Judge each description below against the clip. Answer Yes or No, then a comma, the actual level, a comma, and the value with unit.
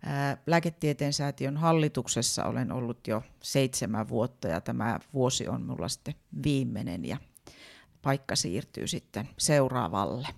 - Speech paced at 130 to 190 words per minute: No, average, 120 wpm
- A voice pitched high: No, low, 135 Hz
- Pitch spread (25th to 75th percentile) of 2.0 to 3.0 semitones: Yes, narrow, 2.6 semitones